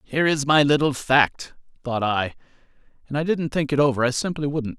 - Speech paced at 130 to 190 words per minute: No, average, 200 wpm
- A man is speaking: Yes, male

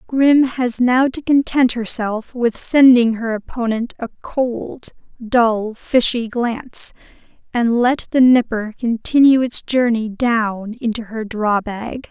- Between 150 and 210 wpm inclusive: No, slow, 135 wpm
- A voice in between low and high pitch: No, high, 235 Hz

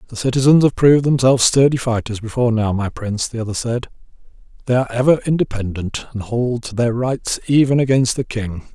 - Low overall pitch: Yes, low, 120 Hz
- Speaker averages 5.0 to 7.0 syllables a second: Yes, 6.0 syllables/s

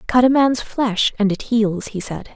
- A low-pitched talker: No, high, 225 Hz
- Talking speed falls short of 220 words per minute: No, fast, 230 wpm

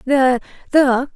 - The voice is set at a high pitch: Yes, very high, 265 Hz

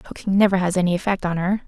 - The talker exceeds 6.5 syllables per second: Yes, 7.5 syllables/s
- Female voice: Yes, female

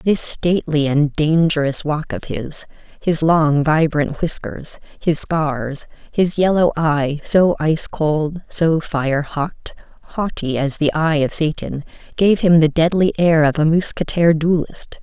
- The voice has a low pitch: No, medium, 155 Hz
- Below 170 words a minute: Yes, average, 150 wpm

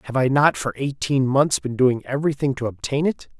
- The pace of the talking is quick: Yes, fast, 210 wpm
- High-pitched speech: No, low, 135 Hz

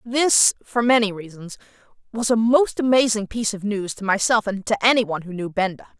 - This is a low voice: No, high, 215 Hz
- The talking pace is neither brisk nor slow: Yes, average, 190 wpm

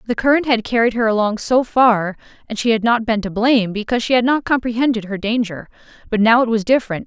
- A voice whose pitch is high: Yes, high, 230 Hz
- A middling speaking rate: No, fast, 230 wpm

